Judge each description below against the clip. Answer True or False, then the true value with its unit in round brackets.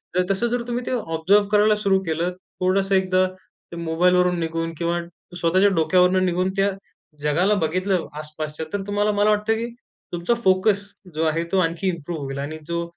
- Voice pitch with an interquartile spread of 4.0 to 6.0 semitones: False (3.3 semitones)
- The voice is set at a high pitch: False (180 Hz)